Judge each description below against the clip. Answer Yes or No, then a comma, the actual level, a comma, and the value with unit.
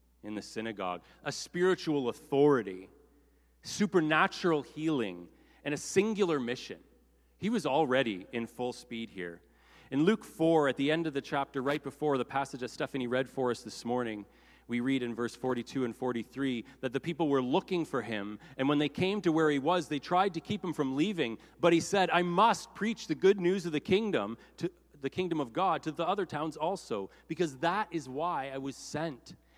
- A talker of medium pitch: Yes, medium, 145 Hz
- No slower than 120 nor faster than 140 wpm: No, average, 195 wpm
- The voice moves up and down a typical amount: No, wide, 6.0 semitones